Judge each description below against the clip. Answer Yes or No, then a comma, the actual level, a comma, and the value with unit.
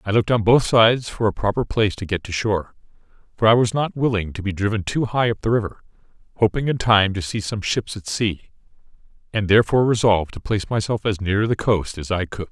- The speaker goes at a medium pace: No, fast, 230 wpm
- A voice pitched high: No, low, 105 Hz